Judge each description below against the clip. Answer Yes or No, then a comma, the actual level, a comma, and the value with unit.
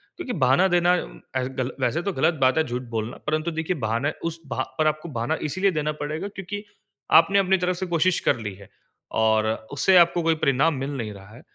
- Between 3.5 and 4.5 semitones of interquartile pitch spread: No, wide, 5.5 semitones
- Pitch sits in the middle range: Yes, medium, 155 Hz